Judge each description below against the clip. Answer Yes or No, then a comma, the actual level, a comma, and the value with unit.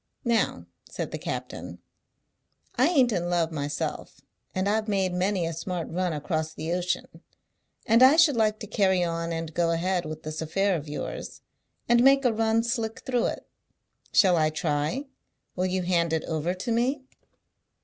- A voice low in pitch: No, medium, 180 Hz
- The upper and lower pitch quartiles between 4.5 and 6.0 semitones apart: Yes, wide, 5.4 semitones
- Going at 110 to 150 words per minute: No, average, 170 wpm